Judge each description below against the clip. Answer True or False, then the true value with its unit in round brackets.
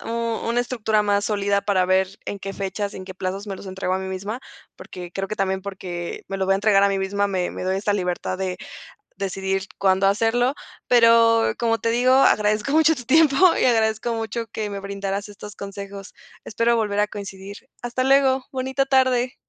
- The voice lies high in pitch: True (205 Hz)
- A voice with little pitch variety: False (3.2 semitones)